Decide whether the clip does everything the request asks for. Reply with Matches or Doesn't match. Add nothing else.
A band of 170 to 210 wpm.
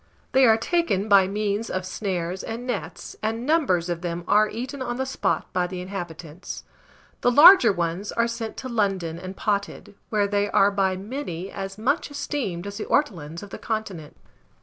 Matches